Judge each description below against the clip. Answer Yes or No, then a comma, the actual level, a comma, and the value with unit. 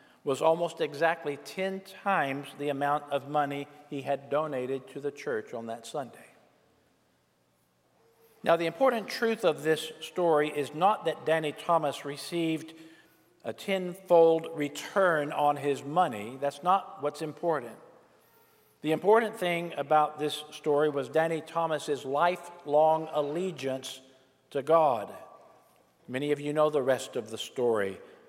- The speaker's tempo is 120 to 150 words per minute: Yes, slow, 135 wpm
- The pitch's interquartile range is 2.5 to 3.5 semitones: Yes, average, 2.9 semitones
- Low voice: No, medium, 150 Hz